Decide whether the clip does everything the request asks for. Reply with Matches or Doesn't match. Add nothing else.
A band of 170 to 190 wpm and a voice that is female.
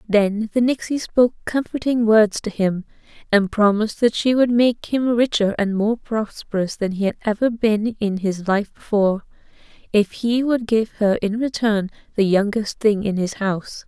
Matches